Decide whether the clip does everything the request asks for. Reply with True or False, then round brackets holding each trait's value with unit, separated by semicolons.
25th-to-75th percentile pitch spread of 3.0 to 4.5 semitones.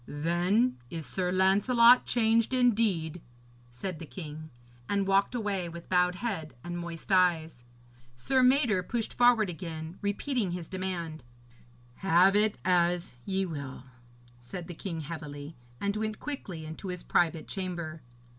True (4.1 semitones)